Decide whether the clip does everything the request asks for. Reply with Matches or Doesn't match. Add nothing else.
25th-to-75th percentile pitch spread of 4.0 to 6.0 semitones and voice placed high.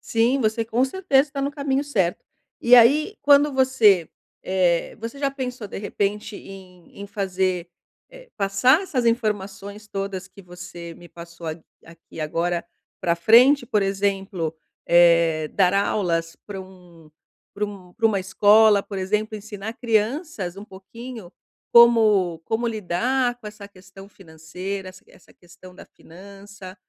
Matches